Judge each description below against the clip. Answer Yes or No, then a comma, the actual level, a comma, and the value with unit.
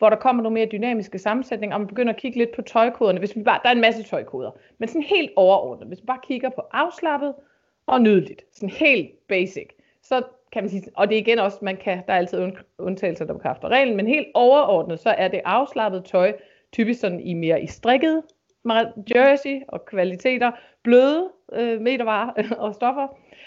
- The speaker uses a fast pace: No, average, 200 wpm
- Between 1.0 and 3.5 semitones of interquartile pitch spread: No, average, 4.3 semitones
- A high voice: Yes, high, 230 Hz